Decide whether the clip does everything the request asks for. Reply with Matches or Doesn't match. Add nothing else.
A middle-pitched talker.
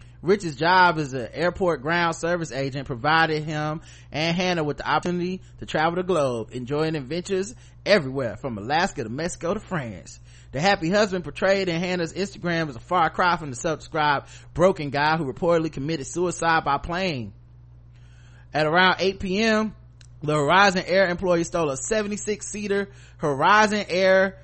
Matches